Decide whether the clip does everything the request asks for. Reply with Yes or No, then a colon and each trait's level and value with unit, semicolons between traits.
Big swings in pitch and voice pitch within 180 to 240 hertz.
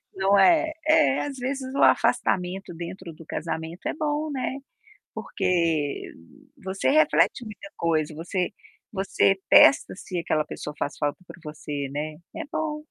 Yes: wide, 8.9 semitones; medium, 185 Hz